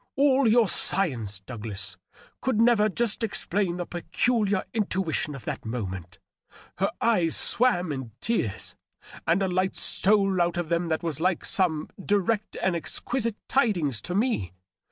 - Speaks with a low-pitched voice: No, medium, 185 Hz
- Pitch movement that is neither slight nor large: No, wide, 5.7 semitones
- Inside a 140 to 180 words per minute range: Yes, average, 150 wpm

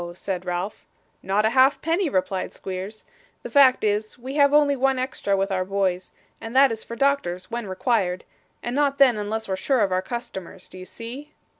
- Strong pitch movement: Yes, wide, 6.0 semitones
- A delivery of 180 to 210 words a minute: Yes, average, 190 wpm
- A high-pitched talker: Yes, high, 220 Hz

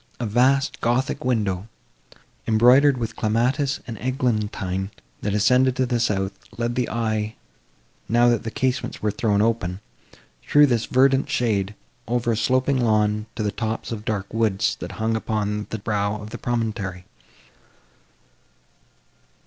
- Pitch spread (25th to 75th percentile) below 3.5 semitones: Yes, average, 2.9 semitones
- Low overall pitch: Yes, low, 115 Hz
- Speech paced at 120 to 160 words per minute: Yes, average, 140 wpm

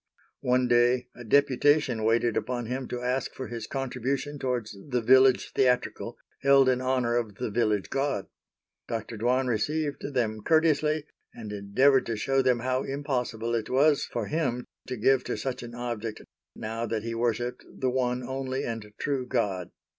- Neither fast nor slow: Yes, average, 165 wpm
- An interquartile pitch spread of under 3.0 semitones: Yes, narrow, 2.4 semitones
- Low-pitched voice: Yes, low, 125 Hz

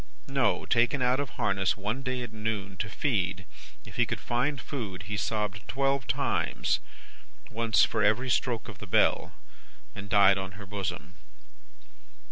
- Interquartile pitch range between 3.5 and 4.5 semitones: Yes, average, 4.1 semitones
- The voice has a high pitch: No, low, 105 Hz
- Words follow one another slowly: No, average, 155 wpm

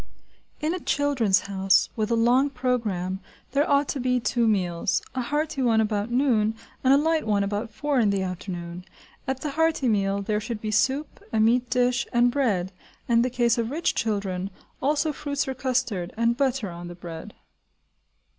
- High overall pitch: Yes, high, 235 Hz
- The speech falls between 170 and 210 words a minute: Yes, average, 185 wpm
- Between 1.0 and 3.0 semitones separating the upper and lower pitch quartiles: No, average, 4.8 semitones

